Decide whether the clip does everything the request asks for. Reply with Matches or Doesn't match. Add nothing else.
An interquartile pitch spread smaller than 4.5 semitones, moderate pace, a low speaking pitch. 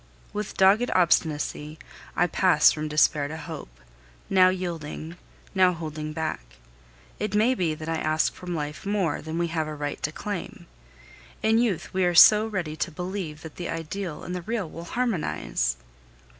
Doesn't match